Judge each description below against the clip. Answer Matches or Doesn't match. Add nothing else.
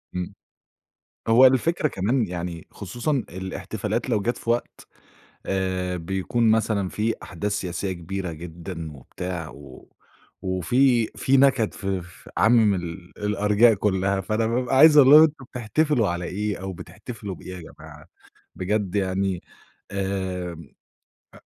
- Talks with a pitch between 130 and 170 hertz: Doesn't match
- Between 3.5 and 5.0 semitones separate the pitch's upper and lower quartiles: Matches